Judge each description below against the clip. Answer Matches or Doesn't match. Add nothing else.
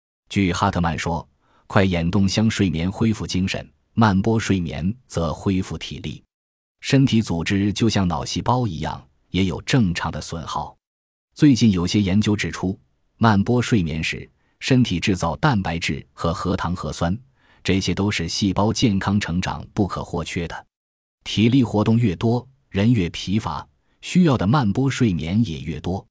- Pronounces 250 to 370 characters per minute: Doesn't match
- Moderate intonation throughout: Matches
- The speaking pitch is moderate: Doesn't match